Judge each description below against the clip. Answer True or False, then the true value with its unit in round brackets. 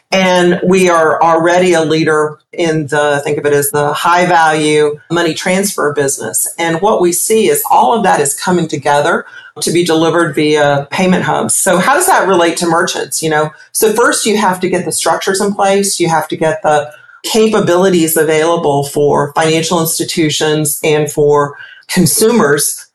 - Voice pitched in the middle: True (165 Hz)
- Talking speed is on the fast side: False (175 wpm)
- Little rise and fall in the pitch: False (3.3 semitones)